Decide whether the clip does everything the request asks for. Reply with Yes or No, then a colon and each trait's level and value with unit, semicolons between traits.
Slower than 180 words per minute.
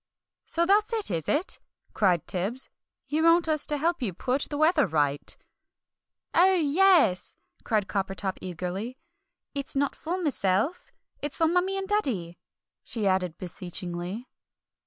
Yes: slow, 135 wpm